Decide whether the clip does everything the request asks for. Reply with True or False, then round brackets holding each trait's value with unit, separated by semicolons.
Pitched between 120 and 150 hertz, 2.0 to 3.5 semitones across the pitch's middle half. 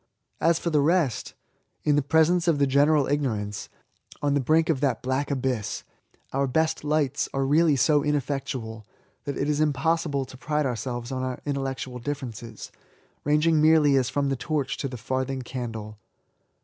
True (140 Hz; 2.7 semitones)